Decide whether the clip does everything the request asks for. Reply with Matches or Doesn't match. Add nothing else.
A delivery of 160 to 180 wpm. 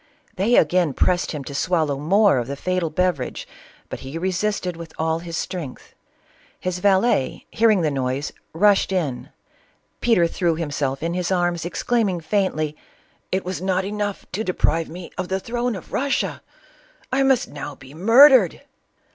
Matches